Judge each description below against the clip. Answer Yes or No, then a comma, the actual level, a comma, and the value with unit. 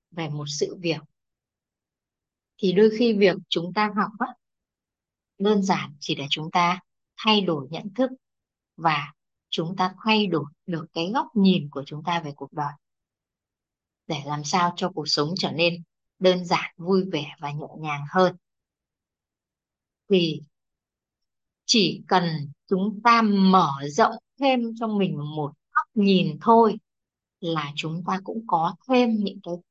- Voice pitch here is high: No, medium, 175 Hz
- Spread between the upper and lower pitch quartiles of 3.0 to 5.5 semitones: Yes, average, 5.1 semitones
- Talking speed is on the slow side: Yes, slow, 150 wpm